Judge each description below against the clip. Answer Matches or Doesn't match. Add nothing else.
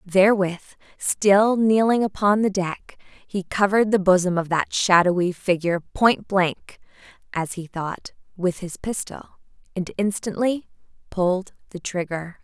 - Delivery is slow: Matches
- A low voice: Doesn't match